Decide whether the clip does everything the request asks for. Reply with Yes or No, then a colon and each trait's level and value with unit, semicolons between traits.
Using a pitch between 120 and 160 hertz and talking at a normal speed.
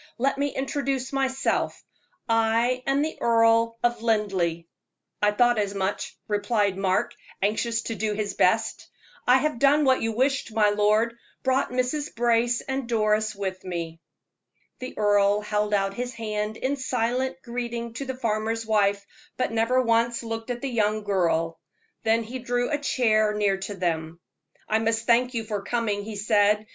No: high, 225 Hz; average, 165 wpm